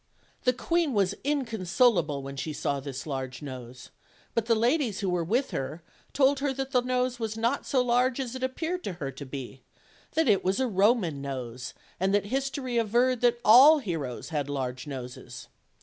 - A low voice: No, high, 215 Hz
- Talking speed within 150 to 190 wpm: Yes, average, 185 wpm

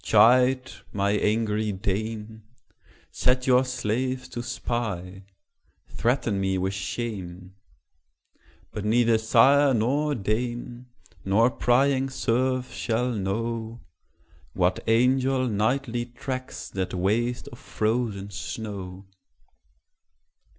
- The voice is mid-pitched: No, low, 115 Hz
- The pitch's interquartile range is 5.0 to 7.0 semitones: No, average, 3.7 semitones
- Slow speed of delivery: Yes, slow, 95 wpm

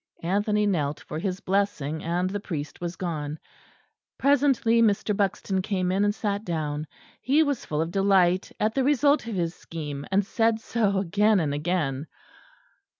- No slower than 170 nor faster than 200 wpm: No, average, 160 wpm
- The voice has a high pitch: Yes, high, 195 Hz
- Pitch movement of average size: Yes, average, 4.4 semitones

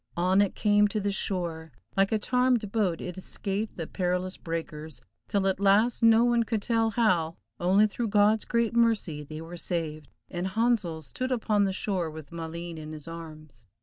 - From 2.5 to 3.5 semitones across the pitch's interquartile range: No, average, 4.7 semitones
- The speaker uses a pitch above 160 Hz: Yes, high, 190 Hz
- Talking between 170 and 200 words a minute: Yes, average, 180 wpm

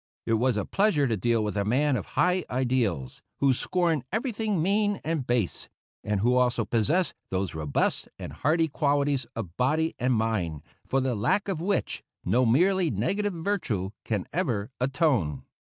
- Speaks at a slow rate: No, average, 165 wpm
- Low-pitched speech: Yes, low, 130 Hz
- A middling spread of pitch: No, wide, 7.4 semitones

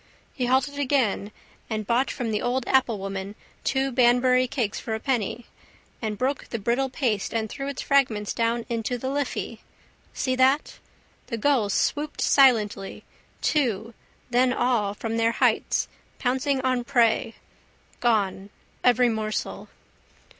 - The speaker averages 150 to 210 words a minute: No, slow, 135 wpm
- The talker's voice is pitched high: Yes, high, 245 Hz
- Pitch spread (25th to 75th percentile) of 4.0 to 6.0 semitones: No, average, 3.2 semitones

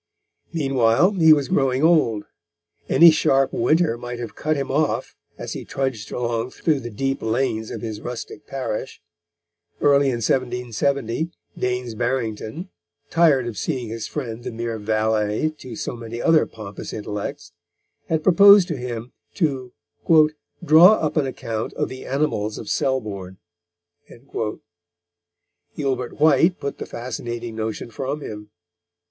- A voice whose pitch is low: Yes, low, 125 Hz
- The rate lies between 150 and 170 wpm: No, slow, 135 wpm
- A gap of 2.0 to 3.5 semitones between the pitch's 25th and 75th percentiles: No, average, 4.4 semitones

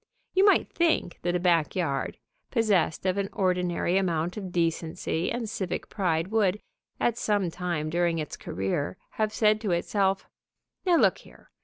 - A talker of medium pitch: Yes, medium, 180 Hz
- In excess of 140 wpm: Yes, average, 160 wpm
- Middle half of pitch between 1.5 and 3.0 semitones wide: No, average, 3.7 semitones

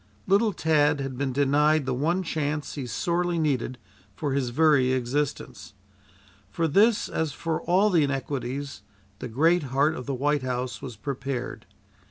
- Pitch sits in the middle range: Yes, medium, 145 Hz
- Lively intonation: No, average, 3.6 semitones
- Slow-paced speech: No, average, 155 wpm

